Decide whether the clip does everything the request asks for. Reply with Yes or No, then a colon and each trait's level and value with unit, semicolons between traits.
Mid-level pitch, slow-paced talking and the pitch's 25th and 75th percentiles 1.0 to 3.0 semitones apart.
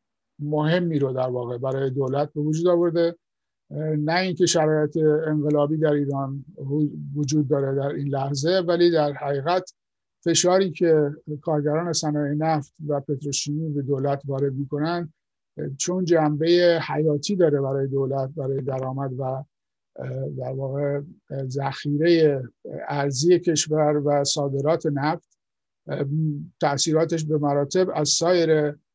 Yes: medium, 150 Hz; slow, 115 wpm; narrow, 2.4 semitones